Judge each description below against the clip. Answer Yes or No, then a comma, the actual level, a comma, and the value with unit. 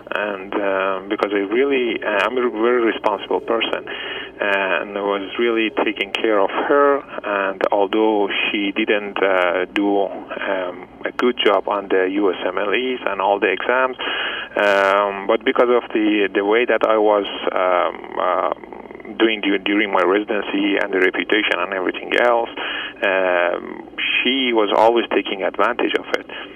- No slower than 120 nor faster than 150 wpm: Yes, average, 145 wpm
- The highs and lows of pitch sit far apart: No, average, 3.6 semitones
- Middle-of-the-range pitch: No, low, 110 Hz